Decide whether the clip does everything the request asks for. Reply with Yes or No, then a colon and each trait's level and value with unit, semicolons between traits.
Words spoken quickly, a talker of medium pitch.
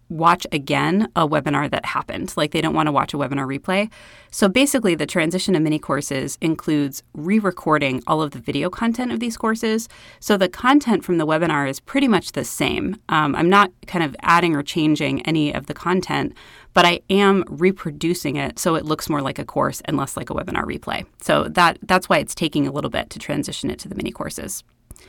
Yes: fast, 215 wpm; medium, 170 Hz